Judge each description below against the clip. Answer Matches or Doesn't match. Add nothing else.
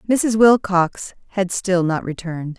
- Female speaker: Matches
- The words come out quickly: Doesn't match